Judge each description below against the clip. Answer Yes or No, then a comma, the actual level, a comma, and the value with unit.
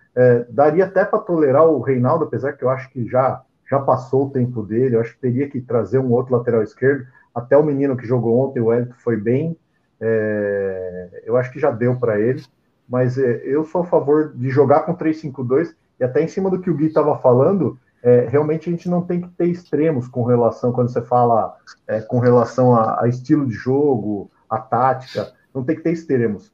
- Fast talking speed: Yes, fast, 215 wpm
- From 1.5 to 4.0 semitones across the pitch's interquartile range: Yes, average, 3.6 semitones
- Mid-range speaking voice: No, low, 130 Hz